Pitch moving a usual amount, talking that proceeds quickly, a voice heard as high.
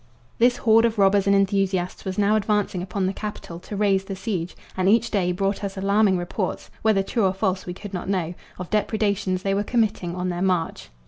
No: narrow, 2.0 semitones; fast, 210 wpm; high, 195 Hz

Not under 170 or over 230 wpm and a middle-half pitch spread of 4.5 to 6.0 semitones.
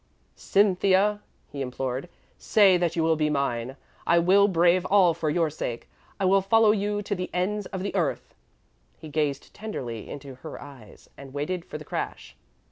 Yes: average, 180 wpm; wide, 5.5 semitones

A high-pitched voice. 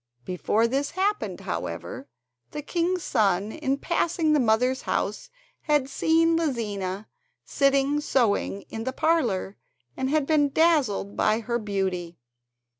Yes: very high, 265 Hz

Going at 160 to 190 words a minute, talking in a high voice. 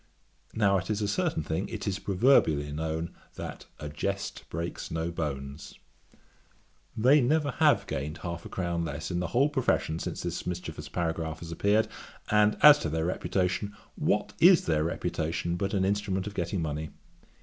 No: average, 170 wpm; very low, 90 Hz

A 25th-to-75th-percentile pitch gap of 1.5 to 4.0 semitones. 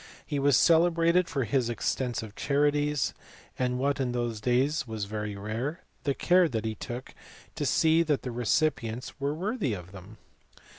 No: average, 5.0 semitones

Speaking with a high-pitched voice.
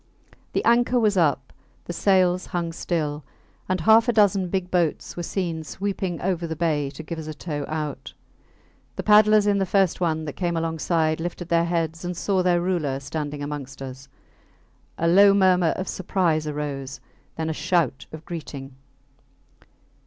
No: medium, 170 Hz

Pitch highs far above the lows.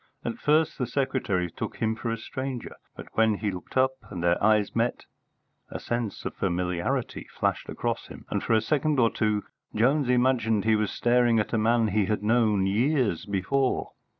No: average, 3.5 semitones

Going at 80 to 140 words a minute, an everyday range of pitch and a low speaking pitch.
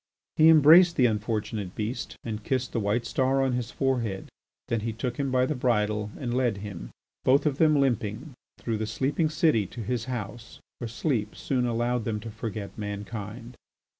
No: average, 180 wpm; average, 3.7 semitones; low, 120 Hz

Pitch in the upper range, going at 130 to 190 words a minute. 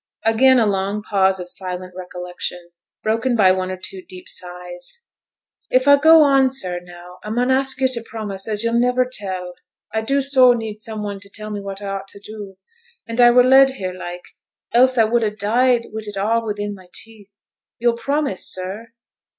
No: high, 215 Hz; average, 200 wpm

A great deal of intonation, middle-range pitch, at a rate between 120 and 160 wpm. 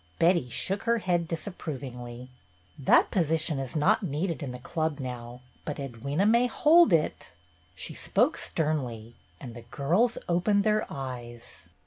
Yes: wide, 6.6 semitones; medium, 150 Hz; average, 140 wpm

